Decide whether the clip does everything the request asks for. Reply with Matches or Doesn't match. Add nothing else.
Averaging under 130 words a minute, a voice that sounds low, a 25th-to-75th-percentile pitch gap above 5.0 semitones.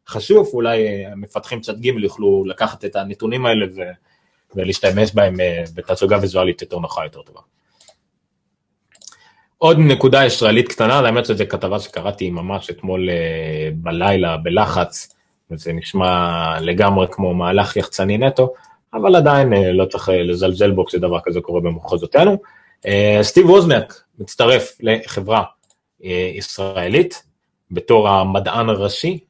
Doesn't match